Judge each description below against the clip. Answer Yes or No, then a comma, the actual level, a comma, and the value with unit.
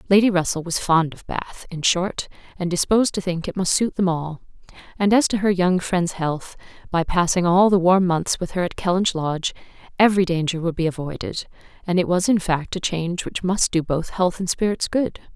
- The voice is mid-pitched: Yes, medium, 180 Hz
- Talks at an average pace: No, fast, 215 wpm